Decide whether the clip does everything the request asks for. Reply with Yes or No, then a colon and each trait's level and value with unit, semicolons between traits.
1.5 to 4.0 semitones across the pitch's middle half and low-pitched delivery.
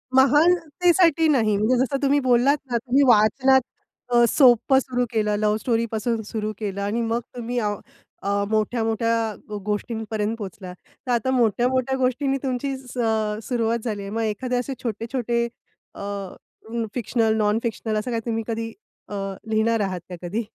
No: average, 3.0 semitones; high, 230 Hz